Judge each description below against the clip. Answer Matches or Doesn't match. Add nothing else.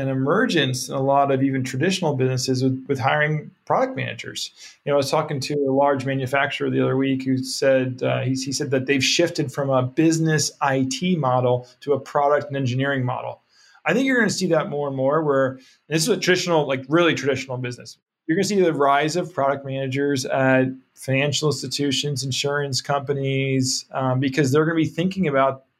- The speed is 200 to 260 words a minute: Matches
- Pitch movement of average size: Doesn't match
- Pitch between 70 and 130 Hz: Doesn't match